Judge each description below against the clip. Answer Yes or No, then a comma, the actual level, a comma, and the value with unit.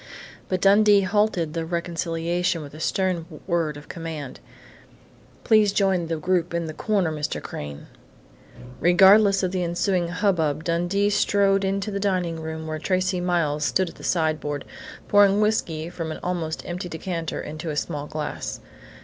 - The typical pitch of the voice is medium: Yes, medium, 175 Hz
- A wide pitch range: No, average, 3.3 semitones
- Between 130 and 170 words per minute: Yes, average, 155 wpm